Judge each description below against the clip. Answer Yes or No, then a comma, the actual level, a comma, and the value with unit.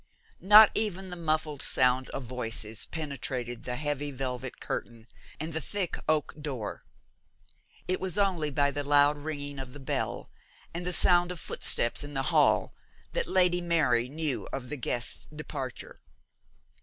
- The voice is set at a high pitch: No, medium, 145 Hz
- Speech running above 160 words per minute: No, average, 155 wpm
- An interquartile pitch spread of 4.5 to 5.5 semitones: Yes, average, 4.8 semitones